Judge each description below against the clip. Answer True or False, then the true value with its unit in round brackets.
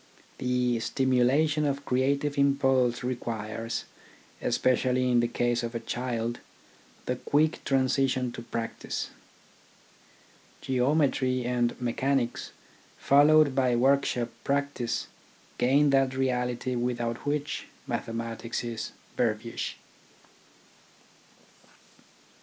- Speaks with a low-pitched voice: True (125 Hz)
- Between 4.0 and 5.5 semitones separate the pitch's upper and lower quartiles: False (2.4 semitones)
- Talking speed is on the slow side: True (95 wpm)